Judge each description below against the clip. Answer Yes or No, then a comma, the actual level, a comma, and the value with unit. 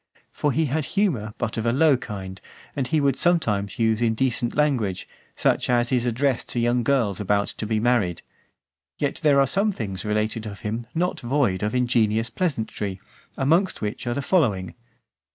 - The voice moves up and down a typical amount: Yes, average, 4.6 semitones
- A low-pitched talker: Yes, low, 120 Hz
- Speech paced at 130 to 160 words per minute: No, average, 175 wpm